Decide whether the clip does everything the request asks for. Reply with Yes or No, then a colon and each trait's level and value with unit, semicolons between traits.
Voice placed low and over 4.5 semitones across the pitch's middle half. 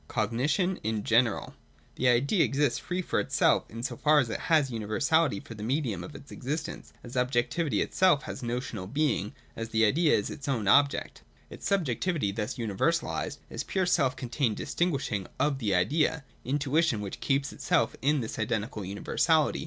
Yes: low, 130 Hz; average, 5.3 semitones